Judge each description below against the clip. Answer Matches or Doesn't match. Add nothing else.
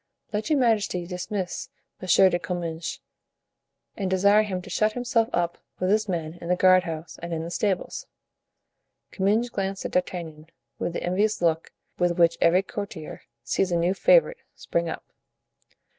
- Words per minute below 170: Matches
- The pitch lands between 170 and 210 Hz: Matches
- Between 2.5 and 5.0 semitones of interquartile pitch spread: Matches